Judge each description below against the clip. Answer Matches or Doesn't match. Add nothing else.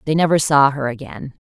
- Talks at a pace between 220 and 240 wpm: Doesn't match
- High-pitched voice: Doesn't match